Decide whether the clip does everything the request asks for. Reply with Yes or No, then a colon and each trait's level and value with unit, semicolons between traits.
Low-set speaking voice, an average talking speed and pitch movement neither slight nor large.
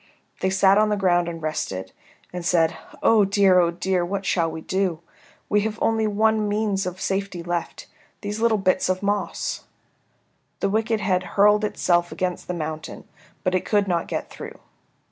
No: high, 190 Hz; average, 175 wpm; average, 3.1 semitones